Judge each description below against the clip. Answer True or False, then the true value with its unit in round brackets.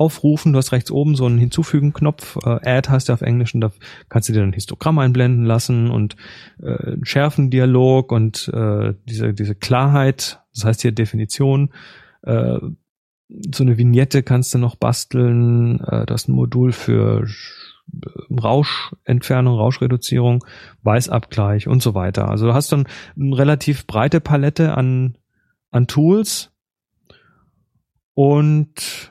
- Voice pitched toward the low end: True (125 Hz)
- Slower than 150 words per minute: True (140 wpm)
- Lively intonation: False (3.4 semitones)